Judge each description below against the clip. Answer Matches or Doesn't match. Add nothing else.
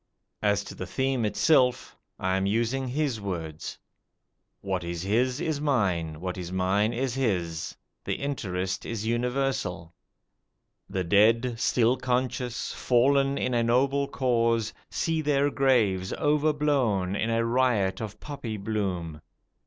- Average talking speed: Doesn't match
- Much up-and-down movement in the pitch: Matches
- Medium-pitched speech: Doesn't match